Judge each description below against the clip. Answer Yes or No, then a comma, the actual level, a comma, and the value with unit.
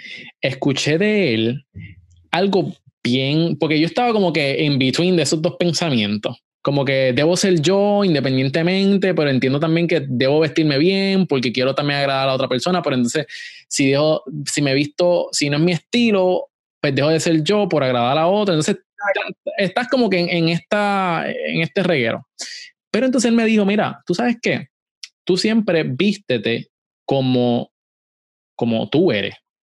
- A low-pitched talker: No, medium, 165 Hz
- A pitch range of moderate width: No, wide, 6.0 semitones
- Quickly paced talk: No, average, 170 wpm